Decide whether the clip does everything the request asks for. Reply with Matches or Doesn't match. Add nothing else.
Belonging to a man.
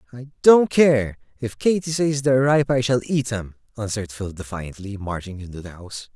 Matches